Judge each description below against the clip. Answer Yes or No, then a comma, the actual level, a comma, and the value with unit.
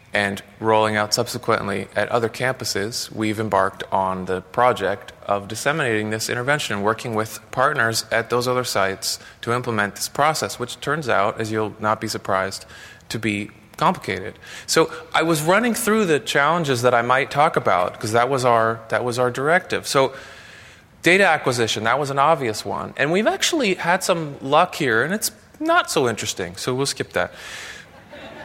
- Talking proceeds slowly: No, average, 175 wpm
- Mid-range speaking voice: No, low, 115 Hz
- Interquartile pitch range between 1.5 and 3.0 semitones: No, average, 4.1 semitones